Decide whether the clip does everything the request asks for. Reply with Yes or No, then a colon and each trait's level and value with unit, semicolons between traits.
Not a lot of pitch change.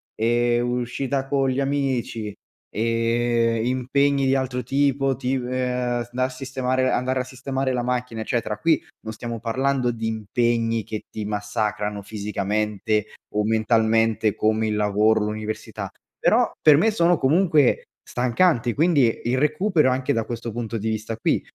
No: average, 3.1 semitones